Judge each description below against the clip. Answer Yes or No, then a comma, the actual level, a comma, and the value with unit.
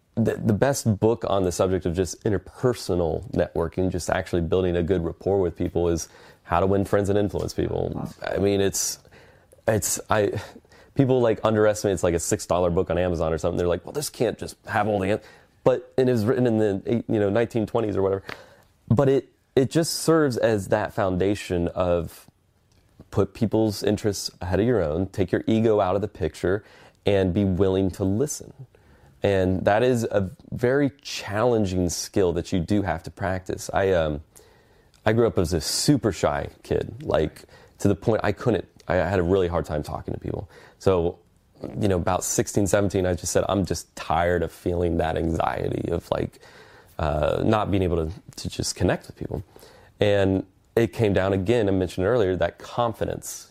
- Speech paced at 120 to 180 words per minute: No, average, 190 wpm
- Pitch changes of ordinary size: Yes, average, 3.5 semitones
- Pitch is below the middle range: Yes, low, 100 Hz